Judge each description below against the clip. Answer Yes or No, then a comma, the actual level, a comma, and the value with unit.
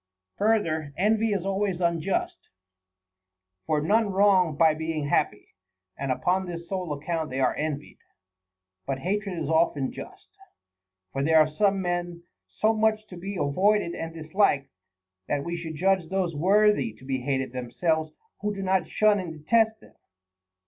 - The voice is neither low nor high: Yes, medium, 170 Hz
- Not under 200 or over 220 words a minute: No, average, 155 wpm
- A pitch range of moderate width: Yes, average, 4.6 semitones